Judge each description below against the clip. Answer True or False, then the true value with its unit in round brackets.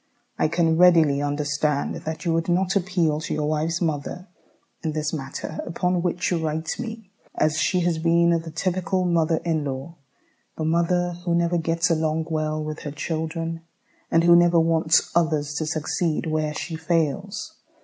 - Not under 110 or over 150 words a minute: False (170 wpm)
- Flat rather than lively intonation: True (1.8 semitones)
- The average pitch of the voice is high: False (165 Hz)